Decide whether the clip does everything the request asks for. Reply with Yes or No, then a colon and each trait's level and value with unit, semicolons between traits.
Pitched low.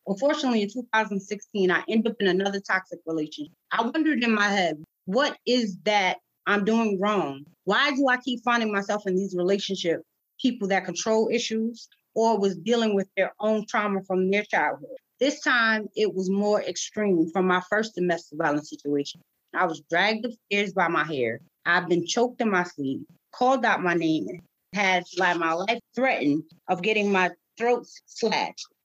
No: high, 200 Hz